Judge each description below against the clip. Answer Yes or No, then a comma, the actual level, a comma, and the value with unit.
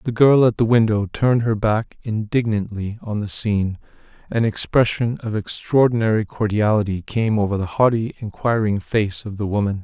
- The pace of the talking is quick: No, average, 160 wpm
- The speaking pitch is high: No, low, 110 Hz